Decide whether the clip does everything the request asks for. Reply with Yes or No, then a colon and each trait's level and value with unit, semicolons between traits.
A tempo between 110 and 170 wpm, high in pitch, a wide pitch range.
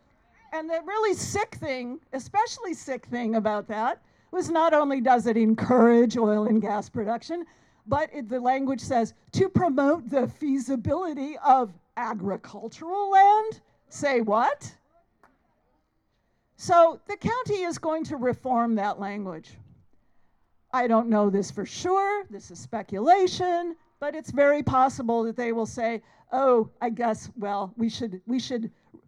Yes: average, 140 wpm; very high, 255 Hz; wide, 6.1 semitones